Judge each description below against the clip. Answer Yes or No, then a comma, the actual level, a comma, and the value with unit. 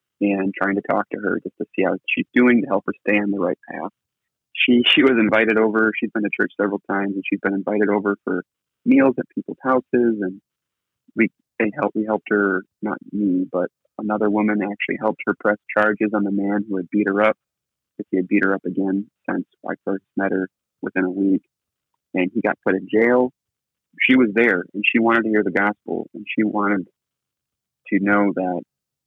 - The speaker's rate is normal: No, fast, 215 wpm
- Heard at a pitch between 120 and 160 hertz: No, low, 105 Hz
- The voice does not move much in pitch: Yes, narrow, 2.0 semitones